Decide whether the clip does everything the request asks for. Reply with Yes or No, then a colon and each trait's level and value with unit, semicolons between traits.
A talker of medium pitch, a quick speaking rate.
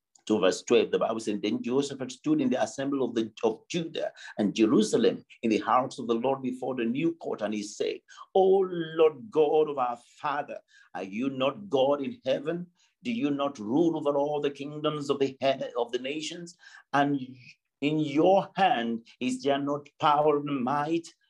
No: medium, 145 Hz; average, 190 wpm